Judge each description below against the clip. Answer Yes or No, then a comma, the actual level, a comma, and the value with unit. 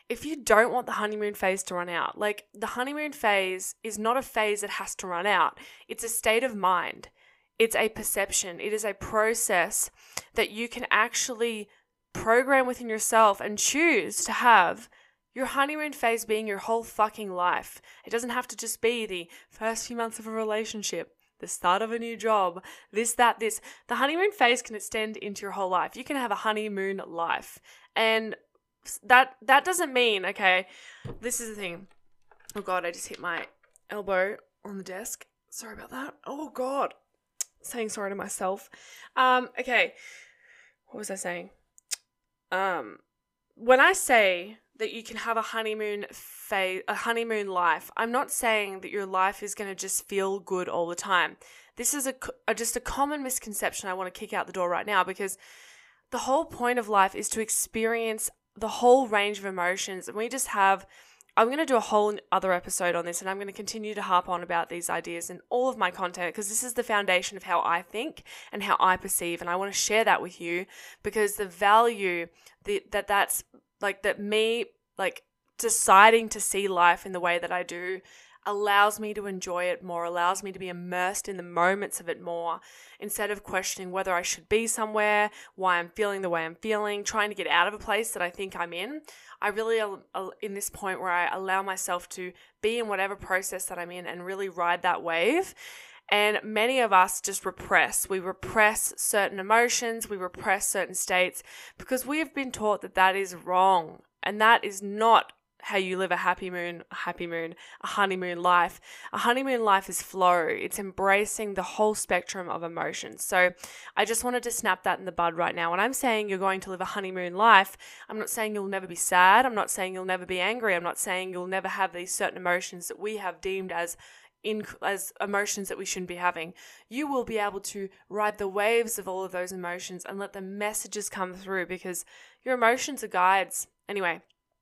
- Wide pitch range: No, average, 3.4 semitones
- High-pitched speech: Yes, high, 205 Hz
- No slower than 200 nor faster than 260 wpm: Yes, fast, 205 wpm